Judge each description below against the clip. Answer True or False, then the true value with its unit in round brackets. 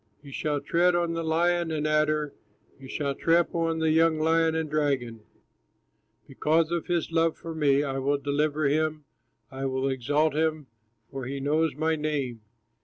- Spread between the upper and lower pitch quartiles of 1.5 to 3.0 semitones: True (2.4 semitones)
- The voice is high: False (155 Hz)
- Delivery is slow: False (170 wpm)